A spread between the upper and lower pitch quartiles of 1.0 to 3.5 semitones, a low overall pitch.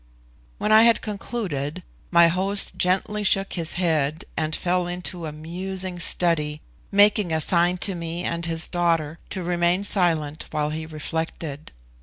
No: average, 2.8 semitones; medium, 175 Hz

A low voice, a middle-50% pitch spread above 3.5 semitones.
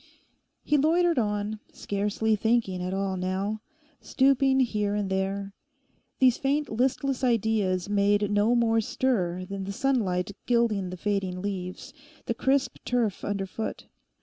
No: high, 210 Hz; average, 4.0 semitones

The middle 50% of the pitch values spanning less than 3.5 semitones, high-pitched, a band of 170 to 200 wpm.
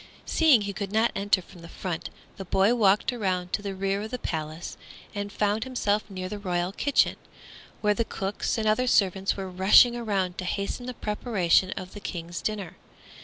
Yes: average, 2.7 semitones; high, 200 Hz; average, 190 wpm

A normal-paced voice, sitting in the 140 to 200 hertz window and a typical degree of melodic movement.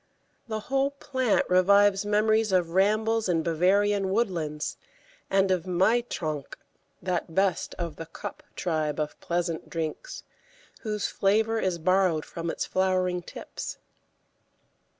No: slow, 125 wpm; high, 190 Hz; average, 3.9 semitones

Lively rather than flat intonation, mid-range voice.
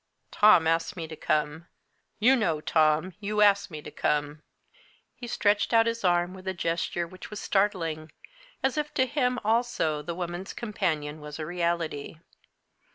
No: average, 5.0 semitones; medium, 175 Hz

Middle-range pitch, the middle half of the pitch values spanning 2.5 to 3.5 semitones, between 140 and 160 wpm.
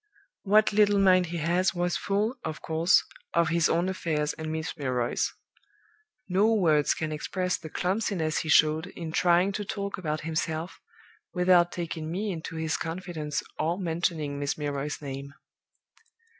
Yes: medium, 170 Hz; average, 3.0 semitones; average, 150 wpm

